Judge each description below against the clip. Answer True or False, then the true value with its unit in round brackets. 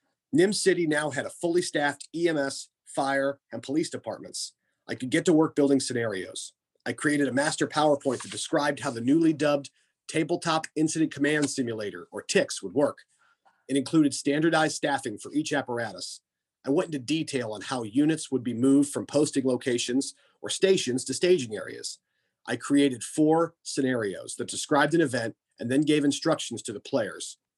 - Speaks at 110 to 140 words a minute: False (170 wpm)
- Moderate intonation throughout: True (3.0 semitones)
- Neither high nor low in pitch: True (145 Hz)